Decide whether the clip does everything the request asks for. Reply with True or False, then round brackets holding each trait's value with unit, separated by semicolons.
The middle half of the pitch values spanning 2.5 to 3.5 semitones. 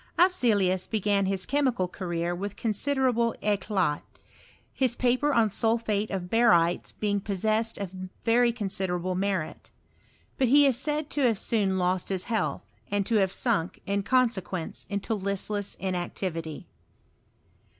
False (3.9 semitones)